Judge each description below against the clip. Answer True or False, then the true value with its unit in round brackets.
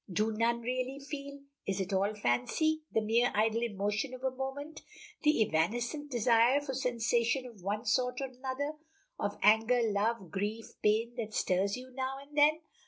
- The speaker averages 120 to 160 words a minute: False (170 wpm)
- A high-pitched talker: True (235 Hz)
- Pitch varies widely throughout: False (3.9 semitones)